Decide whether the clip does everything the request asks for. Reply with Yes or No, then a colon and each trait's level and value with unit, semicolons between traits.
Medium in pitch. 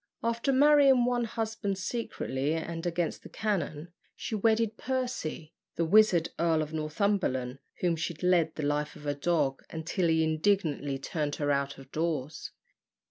Yes: medium, 165 Hz